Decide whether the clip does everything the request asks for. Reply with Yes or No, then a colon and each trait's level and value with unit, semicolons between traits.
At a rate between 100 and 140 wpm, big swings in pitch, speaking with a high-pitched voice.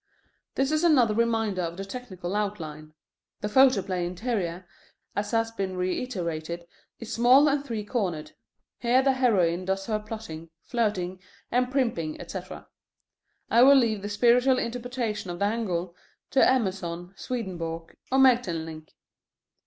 Yes: slow, 135 wpm; wide, 5.7 semitones; high, 210 Hz